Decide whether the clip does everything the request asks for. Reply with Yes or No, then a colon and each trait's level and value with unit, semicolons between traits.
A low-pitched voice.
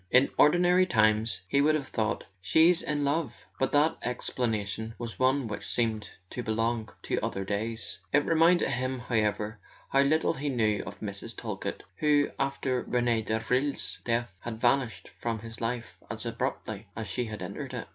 Yes: low, 120 Hz